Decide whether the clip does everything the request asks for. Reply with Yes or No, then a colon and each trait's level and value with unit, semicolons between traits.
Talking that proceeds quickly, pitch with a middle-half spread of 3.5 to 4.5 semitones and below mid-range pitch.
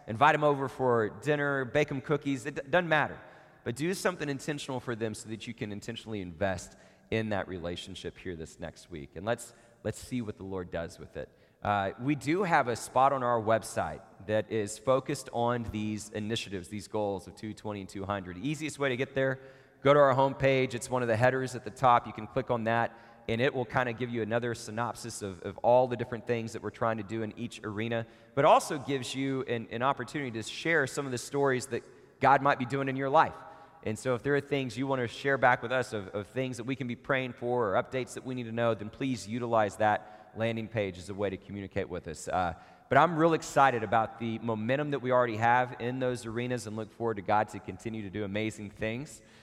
Yes: fast, 235 wpm; average, 3.8 semitones; low, 120 Hz